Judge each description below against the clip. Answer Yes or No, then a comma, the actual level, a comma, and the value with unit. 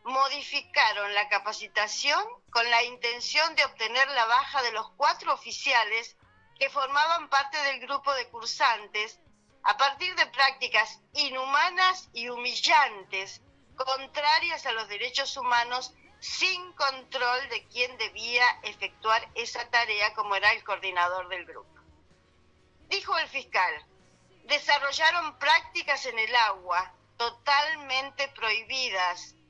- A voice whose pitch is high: Yes, very high, 250 Hz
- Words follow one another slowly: Yes, slow, 115 wpm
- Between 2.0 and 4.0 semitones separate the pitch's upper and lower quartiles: No, average, 4.9 semitones